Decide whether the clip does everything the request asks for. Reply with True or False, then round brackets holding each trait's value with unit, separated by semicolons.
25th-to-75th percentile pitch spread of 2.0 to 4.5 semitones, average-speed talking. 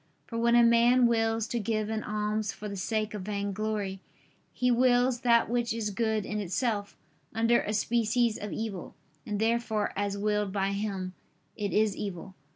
True (2.4 semitones; 170 wpm)